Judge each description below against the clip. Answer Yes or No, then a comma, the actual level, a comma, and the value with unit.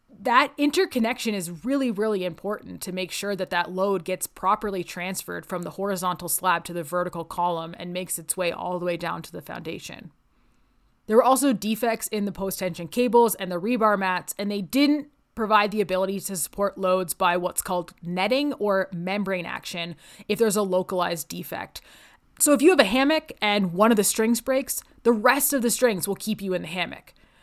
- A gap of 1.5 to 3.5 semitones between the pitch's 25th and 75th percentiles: No, average, 4.1 semitones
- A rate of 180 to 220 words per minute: Yes, average, 200 wpm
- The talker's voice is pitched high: Yes, high, 195 Hz